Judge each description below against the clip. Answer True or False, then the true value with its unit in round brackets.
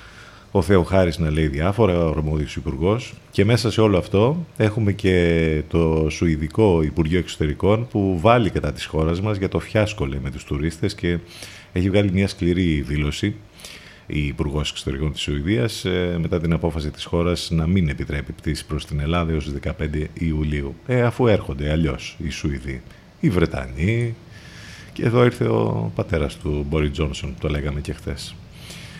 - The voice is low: True (85 Hz)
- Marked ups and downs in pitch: False (4.8 semitones)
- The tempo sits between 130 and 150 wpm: False (165 wpm)